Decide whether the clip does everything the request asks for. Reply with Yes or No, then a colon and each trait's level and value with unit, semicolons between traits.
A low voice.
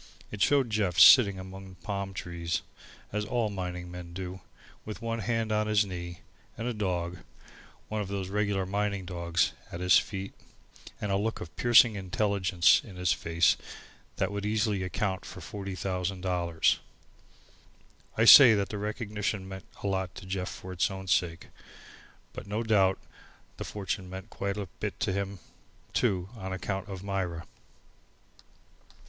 Yes: very low, 95 Hz